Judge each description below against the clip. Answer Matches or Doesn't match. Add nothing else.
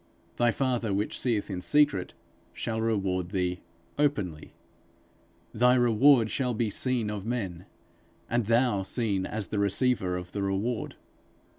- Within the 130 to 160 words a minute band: Matches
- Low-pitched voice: Matches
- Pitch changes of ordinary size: Matches